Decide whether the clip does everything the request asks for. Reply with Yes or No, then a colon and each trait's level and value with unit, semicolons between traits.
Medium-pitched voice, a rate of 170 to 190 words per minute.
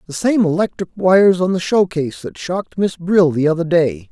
No: medium, 175 Hz; fast, 205 wpm